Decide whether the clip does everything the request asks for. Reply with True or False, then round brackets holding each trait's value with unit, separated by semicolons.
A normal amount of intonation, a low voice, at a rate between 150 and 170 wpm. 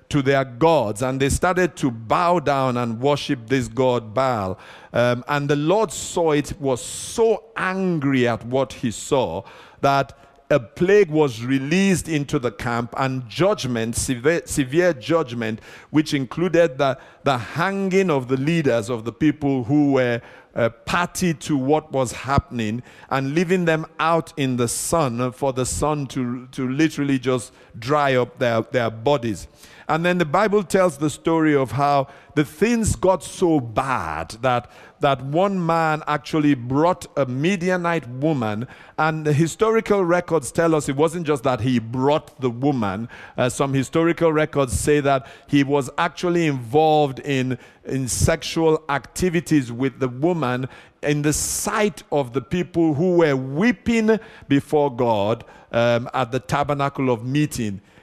False (4.3 semitones; 145 Hz; 155 wpm)